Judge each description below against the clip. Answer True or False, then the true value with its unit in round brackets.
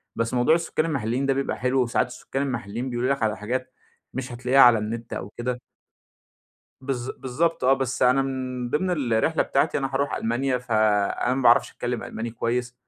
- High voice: False (125 Hz)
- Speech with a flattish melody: True (2.3 semitones)